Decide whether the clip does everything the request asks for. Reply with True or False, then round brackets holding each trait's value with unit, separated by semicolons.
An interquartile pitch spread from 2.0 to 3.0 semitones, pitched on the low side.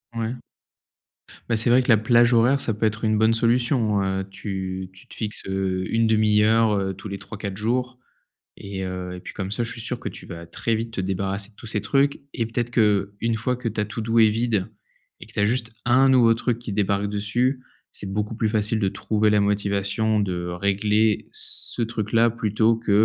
True (2.5 semitones; 110 Hz)